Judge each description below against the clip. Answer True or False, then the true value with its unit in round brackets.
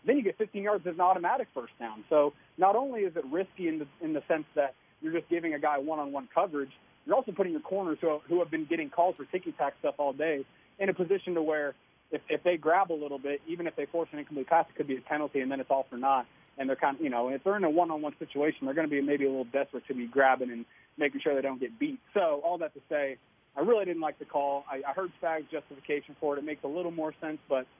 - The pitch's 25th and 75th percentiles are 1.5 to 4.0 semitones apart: True (3.7 semitones)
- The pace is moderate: False (290 wpm)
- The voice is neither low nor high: True (155 Hz)